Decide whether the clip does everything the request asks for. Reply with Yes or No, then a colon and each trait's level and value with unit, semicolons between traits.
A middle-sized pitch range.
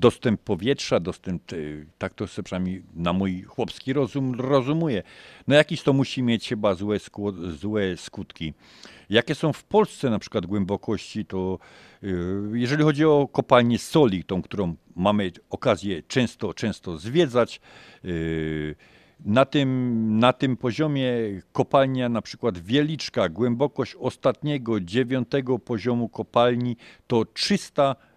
No: wide, 5.7 semitones